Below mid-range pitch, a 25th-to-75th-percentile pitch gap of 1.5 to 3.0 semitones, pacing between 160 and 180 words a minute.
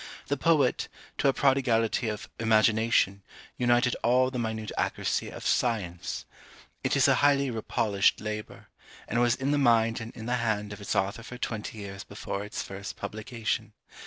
Yes: low, 115 Hz; average, 2.7 semitones; average, 165 wpm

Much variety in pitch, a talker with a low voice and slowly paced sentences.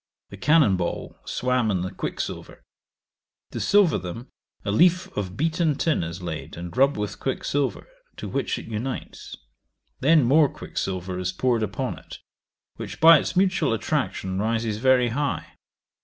No: wide, 7.3 semitones; low, 120 Hz; average, 150 wpm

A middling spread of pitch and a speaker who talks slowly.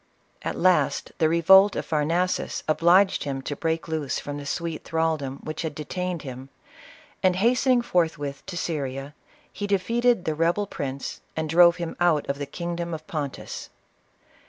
No: average, 3.7 semitones; average, 155 wpm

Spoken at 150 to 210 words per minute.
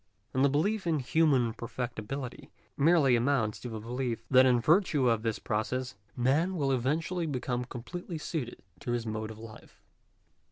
Yes: average, 160 wpm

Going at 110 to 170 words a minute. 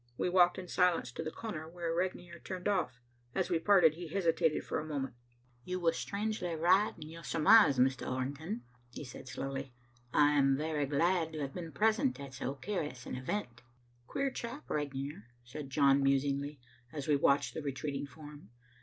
No: average, 180 wpm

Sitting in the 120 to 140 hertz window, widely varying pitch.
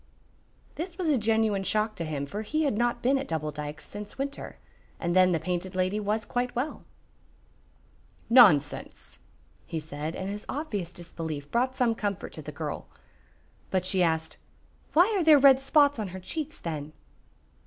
No: high, 205 Hz; wide, 7.7 semitones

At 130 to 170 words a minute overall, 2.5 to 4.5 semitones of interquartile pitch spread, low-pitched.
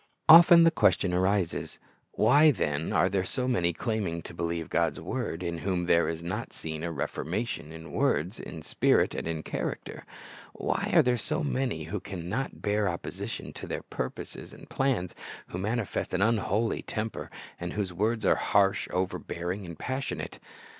No: average, 165 wpm; average, 5.2 semitones; very low, 95 Hz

